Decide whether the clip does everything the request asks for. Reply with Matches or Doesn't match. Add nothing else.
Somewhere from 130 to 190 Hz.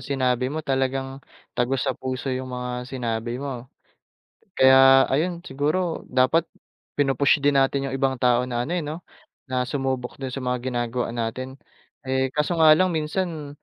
Matches